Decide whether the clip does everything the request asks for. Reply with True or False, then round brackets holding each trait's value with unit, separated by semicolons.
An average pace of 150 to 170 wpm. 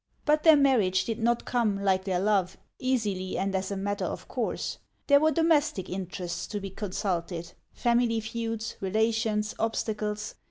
True (160 wpm)